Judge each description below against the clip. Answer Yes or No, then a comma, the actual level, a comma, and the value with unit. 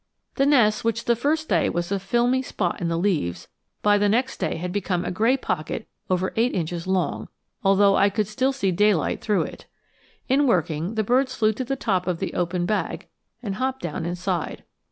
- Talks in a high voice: Yes, high, 200 Hz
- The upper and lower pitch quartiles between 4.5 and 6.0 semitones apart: Yes, average, 5.1 semitones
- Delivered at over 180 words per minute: Yes, average, 200 wpm